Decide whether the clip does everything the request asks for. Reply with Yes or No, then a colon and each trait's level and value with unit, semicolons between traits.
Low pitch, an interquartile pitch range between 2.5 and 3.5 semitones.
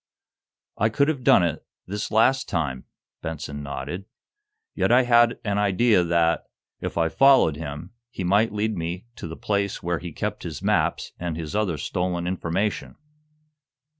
No: very low, 90 Hz; average, 4.6 semitones